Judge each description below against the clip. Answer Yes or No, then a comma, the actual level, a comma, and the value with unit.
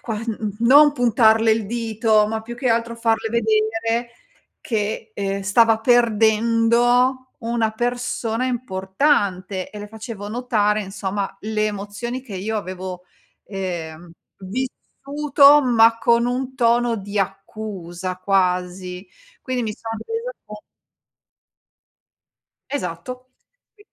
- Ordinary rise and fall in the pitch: Yes, average, 3.0 semitones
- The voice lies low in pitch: No, high, 225 Hz